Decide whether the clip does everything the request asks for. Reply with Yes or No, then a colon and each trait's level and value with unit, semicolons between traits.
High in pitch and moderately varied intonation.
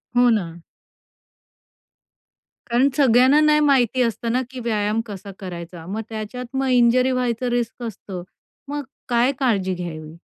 Yes: high, 235 Hz; average, 4.0 semitones